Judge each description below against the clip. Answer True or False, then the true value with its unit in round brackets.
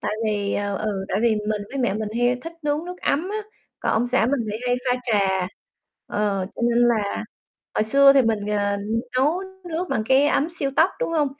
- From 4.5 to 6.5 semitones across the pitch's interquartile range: True (5.0 semitones)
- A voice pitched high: True (235 Hz)